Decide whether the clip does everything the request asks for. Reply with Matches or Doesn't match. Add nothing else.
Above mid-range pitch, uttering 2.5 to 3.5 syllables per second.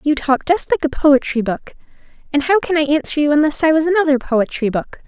Doesn't match